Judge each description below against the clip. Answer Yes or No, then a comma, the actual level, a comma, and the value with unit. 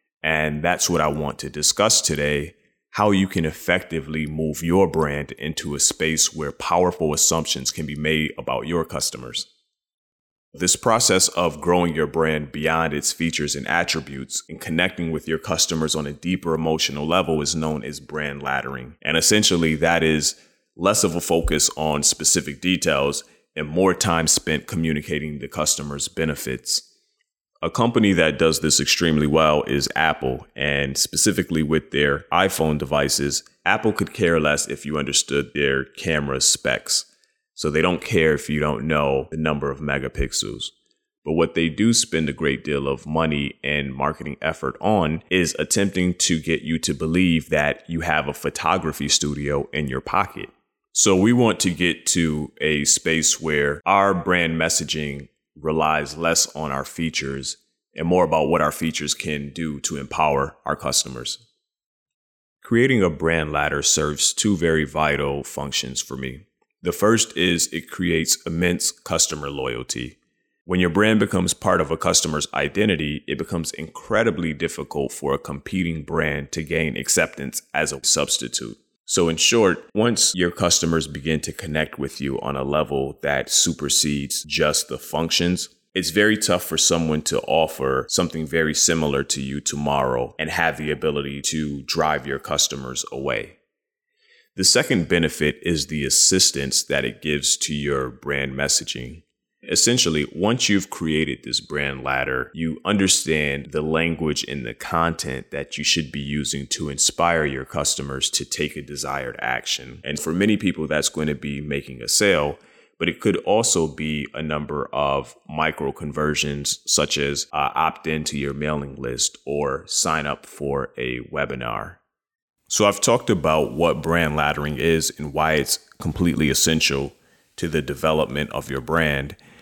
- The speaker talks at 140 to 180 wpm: Yes, average, 160 wpm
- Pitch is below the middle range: Yes, very low, 75 Hz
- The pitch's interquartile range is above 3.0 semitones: No, narrow, 2.6 semitones